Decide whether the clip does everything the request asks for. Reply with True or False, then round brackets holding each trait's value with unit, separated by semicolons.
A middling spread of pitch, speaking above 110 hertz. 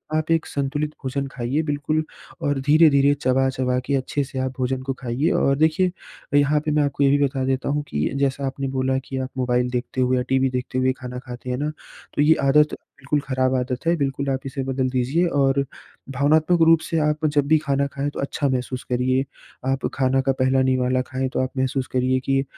False (1.9 semitones; 135 Hz)